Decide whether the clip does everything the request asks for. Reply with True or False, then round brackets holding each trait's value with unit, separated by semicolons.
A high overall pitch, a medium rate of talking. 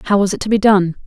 False (200 Hz; 335 wpm)